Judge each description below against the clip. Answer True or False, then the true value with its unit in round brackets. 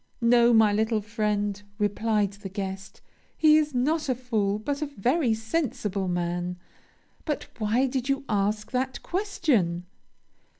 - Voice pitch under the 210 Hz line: False (220 Hz)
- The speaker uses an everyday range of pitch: True (4.5 semitones)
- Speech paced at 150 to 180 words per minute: False (135 wpm)